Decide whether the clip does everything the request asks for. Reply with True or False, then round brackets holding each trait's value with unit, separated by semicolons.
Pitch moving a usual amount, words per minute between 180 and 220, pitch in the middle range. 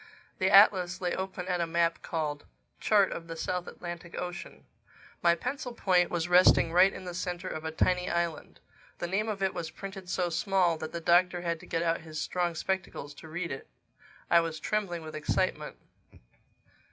False (1.9 semitones; 190 wpm; 175 Hz)